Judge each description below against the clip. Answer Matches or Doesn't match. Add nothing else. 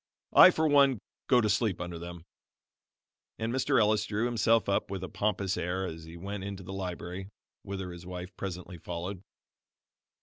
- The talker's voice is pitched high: Doesn't match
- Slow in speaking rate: Doesn't match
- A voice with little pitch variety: Doesn't match